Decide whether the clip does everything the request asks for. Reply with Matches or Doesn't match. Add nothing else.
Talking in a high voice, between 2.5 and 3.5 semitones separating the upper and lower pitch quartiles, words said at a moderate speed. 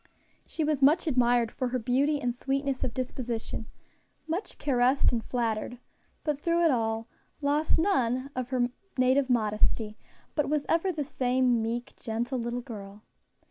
Matches